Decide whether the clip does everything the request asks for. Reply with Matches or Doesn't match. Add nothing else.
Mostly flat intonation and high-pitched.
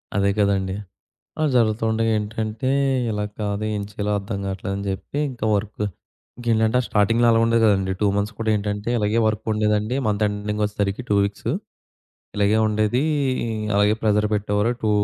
Doesn't match